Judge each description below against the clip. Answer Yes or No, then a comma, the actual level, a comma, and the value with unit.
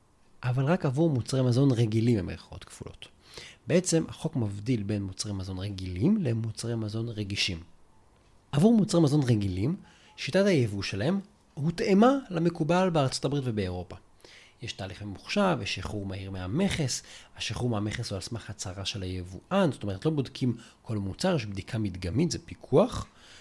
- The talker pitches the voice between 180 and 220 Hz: No, low, 115 Hz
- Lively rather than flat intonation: Yes, wide, 8.0 semitones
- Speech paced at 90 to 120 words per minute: No, average, 145 wpm